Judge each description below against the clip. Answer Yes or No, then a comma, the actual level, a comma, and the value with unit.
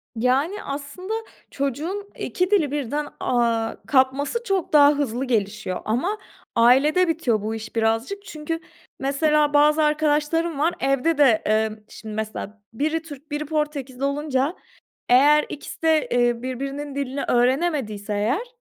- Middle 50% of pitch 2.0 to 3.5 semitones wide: No, average, 4.1 semitones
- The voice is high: Yes, very high, 280 Hz